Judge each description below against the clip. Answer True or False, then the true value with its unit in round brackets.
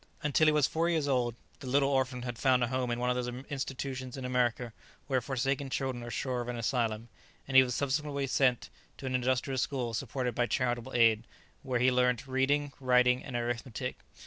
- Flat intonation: True (1.8 semitones)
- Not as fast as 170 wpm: False (200 wpm)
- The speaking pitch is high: False (125 Hz)